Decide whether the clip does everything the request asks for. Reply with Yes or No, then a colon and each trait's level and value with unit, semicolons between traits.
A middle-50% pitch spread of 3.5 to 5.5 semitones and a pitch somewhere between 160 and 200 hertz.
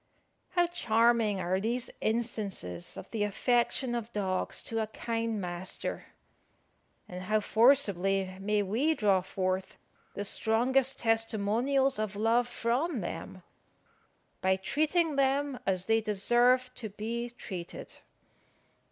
No: average, 4.0 semitones; high, 225 Hz